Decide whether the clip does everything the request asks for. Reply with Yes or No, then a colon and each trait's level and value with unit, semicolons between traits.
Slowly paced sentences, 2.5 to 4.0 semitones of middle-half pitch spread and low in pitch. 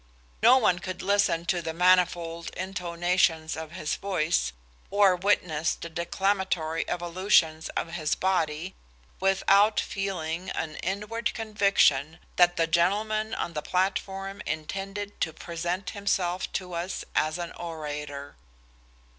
No: slow, 120 wpm; average, 3.0 semitones; medium, 175 Hz